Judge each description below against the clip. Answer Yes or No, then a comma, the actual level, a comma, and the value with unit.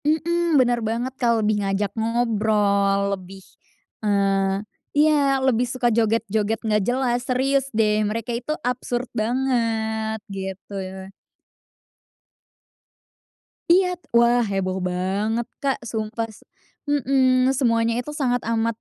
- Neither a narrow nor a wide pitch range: Yes, average, 3.6 semitones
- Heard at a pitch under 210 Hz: No, high, 230 Hz